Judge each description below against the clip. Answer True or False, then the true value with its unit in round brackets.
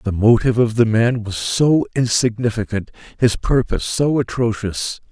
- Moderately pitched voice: False (115 Hz)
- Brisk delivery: False (140 wpm)